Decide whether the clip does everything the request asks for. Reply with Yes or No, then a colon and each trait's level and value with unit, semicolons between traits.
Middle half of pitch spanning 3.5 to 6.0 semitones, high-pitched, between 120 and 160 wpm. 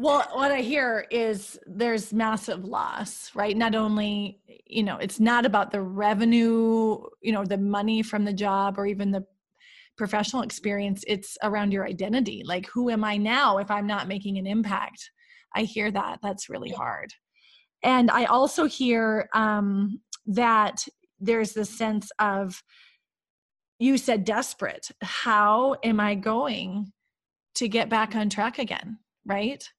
No: average, 2.7 semitones; high, 215 Hz; average, 150 wpm